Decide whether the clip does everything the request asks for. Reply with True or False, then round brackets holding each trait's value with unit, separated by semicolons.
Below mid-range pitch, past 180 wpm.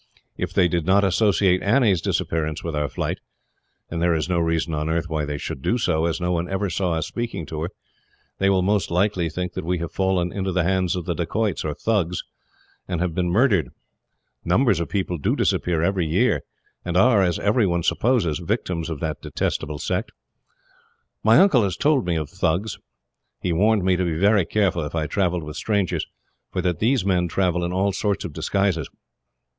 True (90 Hz; 200 wpm)